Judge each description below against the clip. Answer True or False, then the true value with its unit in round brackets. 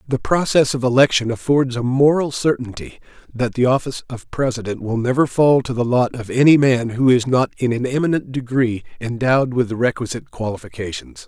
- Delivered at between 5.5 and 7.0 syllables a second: True (5.6 syllables/s)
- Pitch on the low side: True (125 Hz)